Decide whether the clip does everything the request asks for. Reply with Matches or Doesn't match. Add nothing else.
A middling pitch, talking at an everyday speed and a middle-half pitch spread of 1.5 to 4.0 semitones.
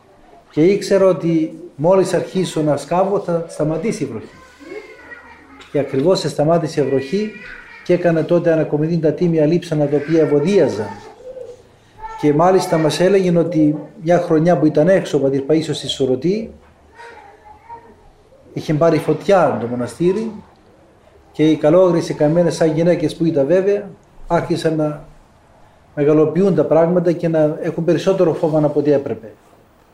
Matches